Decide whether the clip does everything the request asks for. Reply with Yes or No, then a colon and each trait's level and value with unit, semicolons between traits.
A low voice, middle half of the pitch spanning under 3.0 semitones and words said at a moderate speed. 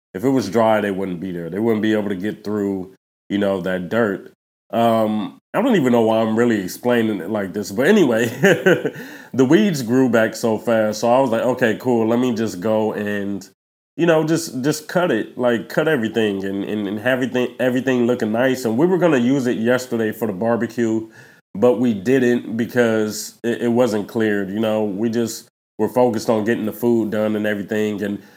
No: low, 110 Hz; narrow, 2.4 semitones; fast, 210 wpm